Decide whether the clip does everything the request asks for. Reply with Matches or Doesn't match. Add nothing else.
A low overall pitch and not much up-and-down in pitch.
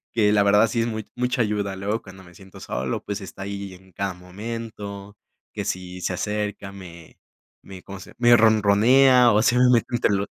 Doesn't match